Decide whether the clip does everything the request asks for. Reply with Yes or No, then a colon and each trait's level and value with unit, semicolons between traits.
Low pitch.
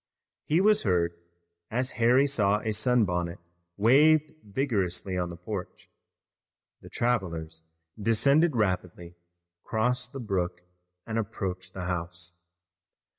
Yes: low, 105 Hz